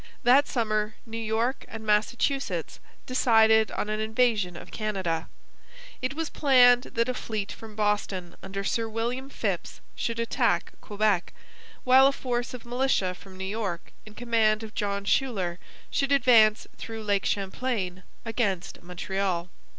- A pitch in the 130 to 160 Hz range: No, high, 220 Hz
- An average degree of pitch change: Yes, average, 3.5 semitones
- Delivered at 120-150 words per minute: Yes, average, 145 wpm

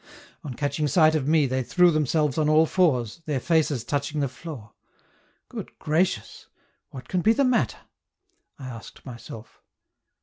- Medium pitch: Yes, medium, 150 Hz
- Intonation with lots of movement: No, average, 3.7 semitones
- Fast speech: No, average, 155 wpm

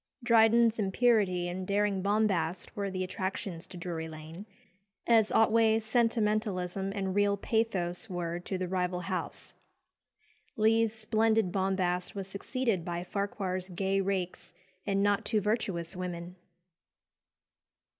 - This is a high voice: Yes, high, 195 Hz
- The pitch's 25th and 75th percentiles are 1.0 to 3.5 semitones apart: Yes, average, 3.2 semitones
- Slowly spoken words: Yes, slow, 125 wpm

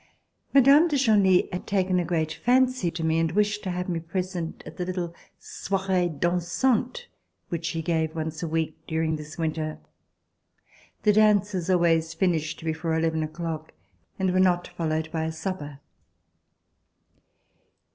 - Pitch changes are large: No, average, 2.9 semitones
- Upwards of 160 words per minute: No, average, 145 wpm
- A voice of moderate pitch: Yes, medium, 170 Hz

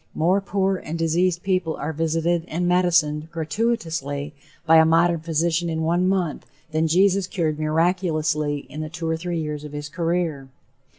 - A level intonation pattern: Yes, narrow, 2.2 semitones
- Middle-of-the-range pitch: Yes, medium, 165 Hz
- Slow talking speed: No, average, 165 wpm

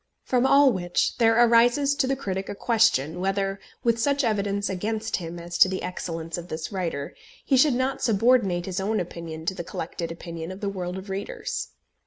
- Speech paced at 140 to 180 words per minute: No, average, 195 wpm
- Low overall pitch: No, high, 195 Hz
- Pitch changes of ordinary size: Yes, average, 4.9 semitones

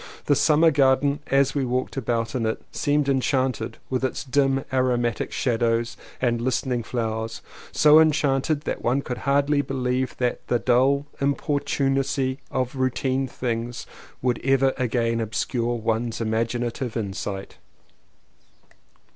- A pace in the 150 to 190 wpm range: No, average, 140 wpm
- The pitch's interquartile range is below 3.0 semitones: Yes, narrow, 2.6 semitones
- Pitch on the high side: No, low, 130 Hz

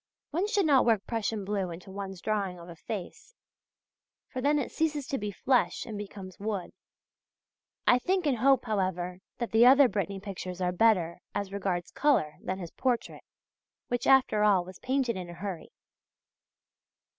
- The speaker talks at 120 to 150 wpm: No, average, 170 wpm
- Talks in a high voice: Yes, high, 205 Hz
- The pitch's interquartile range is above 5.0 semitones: Yes, wide, 5.4 semitones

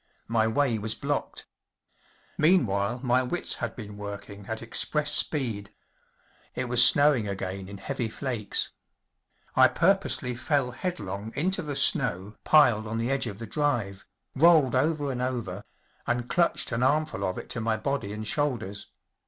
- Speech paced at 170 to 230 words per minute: No, average, 155 wpm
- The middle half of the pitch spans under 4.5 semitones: No, wide, 5.5 semitones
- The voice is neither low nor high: No, low, 120 Hz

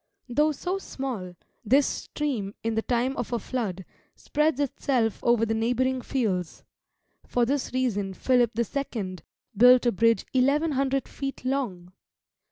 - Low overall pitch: No, high, 245 Hz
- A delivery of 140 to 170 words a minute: Yes, average, 145 wpm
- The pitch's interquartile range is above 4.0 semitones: No, average, 3.5 semitones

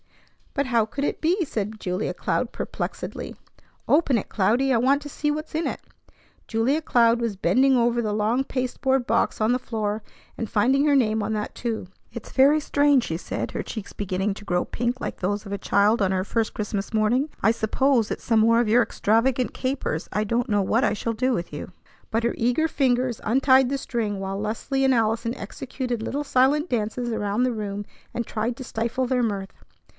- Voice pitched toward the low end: No, high, 235 Hz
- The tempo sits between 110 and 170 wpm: No, average, 200 wpm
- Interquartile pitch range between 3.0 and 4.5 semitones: Yes, average, 3.6 semitones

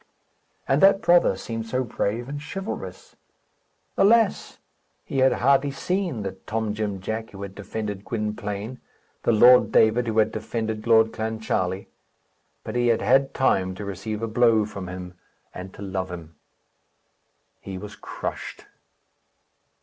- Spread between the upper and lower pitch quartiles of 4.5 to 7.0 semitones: No, average, 3.6 semitones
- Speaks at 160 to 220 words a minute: No, average, 140 wpm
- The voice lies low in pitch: Yes, low, 110 Hz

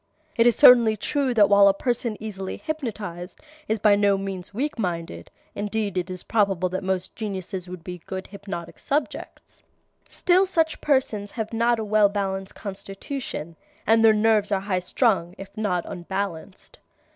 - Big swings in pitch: No, average, 3.0 semitones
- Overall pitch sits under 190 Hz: No, high, 205 Hz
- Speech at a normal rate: Yes, average, 160 wpm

